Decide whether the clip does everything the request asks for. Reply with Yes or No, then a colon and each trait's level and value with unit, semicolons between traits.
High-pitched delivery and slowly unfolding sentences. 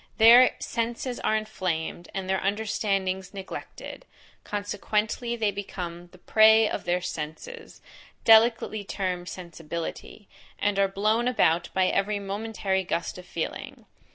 Yes: high, 200 Hz; slow, 125 wpm